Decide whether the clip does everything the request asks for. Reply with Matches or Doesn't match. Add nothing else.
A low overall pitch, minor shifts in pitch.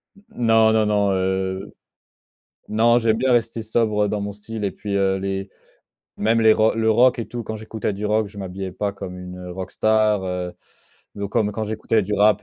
Matches